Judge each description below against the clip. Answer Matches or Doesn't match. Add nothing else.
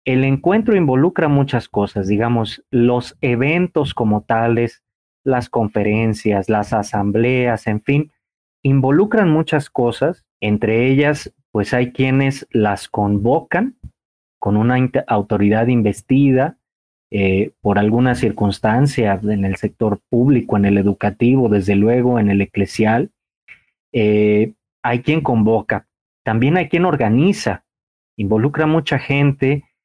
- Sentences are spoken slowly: Matches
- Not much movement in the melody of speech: Doesn't match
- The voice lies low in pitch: Matches